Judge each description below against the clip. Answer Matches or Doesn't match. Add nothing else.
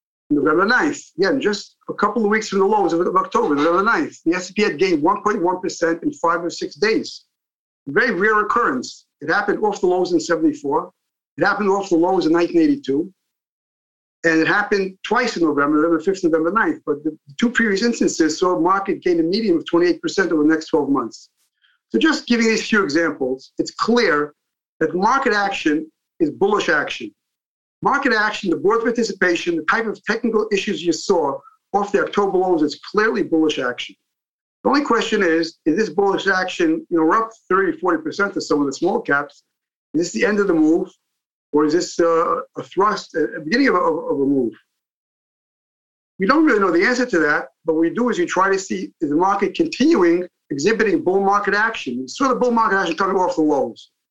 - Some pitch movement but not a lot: Doesn't match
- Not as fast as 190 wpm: Doesn't match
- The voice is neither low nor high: Doesn't match